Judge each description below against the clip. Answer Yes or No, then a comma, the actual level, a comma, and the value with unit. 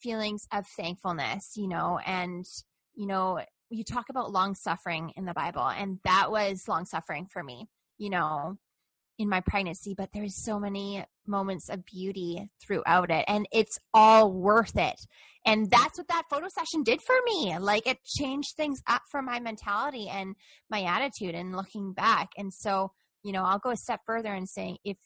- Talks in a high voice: Yes, high, 200 Hz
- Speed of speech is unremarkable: Yes, average, 185 wpm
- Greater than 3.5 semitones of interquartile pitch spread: No, average, 3.1 semitones